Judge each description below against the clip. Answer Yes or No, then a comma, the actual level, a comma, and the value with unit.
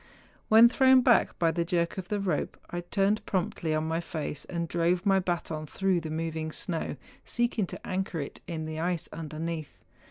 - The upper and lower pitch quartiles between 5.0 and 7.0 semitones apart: No, average, 3.2 semitones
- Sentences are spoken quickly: No, average, 185 wpm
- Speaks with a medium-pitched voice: Yes, medium, 170 Hz